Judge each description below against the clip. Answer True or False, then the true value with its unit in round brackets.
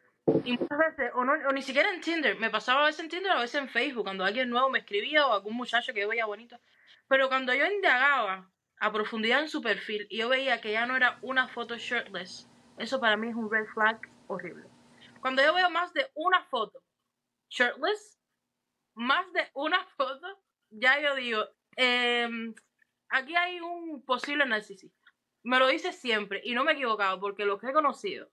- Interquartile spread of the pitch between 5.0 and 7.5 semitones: True (5.3 semitones)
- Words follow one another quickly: True (200 wpm)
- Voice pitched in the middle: False (255 Hz)